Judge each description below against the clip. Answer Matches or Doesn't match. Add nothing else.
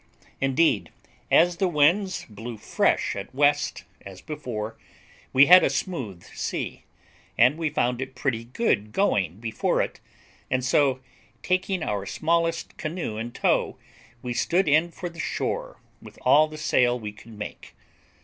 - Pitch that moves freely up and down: Matches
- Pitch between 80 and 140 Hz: Matches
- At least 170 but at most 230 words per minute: Doesn't match